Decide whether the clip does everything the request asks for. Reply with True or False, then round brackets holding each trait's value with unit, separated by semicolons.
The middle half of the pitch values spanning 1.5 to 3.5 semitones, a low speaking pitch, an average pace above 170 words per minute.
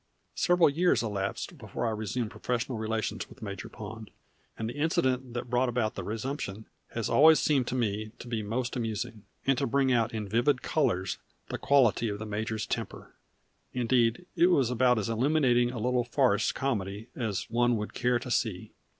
True (2.9 semitones; 120 Hz; 180 wpm)